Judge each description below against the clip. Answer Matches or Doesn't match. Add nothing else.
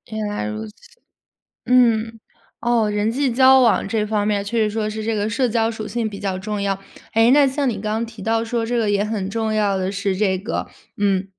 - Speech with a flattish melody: Matches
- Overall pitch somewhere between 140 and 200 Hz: Doesn't match